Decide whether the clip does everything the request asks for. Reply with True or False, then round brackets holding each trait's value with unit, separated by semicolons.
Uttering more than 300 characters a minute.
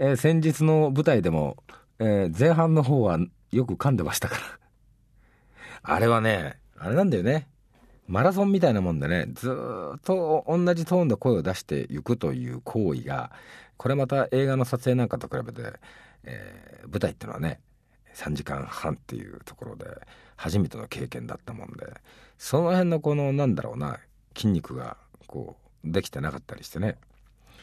True (325 characters per minute)